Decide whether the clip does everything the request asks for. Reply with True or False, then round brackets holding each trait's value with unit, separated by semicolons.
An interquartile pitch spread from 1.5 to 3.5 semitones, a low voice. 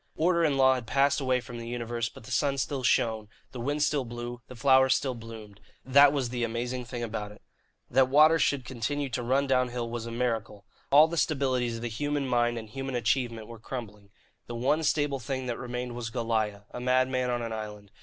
True (2.5 semitones; 125 Hz)